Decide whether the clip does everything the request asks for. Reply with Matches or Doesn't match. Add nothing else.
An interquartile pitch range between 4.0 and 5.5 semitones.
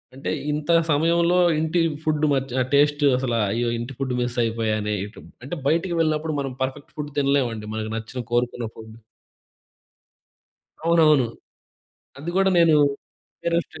Matches